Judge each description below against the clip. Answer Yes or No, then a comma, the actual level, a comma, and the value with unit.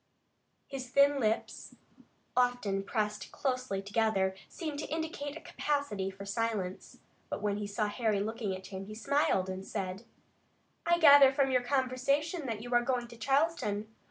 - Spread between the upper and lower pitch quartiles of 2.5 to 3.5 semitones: No, wide, 5.4 semitones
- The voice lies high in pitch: Yes, high, 240 Hz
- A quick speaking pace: No, average, 155 wpm